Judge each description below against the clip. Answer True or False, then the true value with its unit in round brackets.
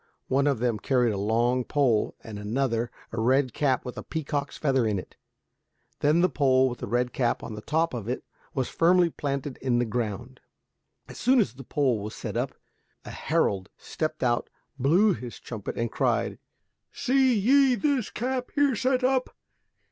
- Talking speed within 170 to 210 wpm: True (180 wpm)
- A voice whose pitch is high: False (130 Hz)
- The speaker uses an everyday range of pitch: False (6.1 semitones)